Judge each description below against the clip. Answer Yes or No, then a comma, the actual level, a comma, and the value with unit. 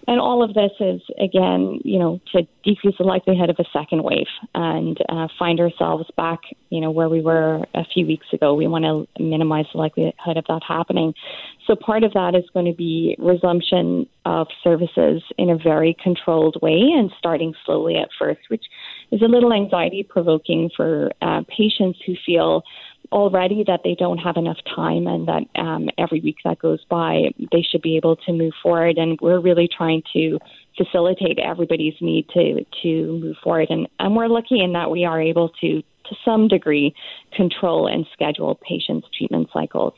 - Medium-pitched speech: Yes, medium, 170 Hz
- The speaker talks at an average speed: Yes, average, 185 wpm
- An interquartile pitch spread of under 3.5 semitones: Yes, narrow, 2.6 semitones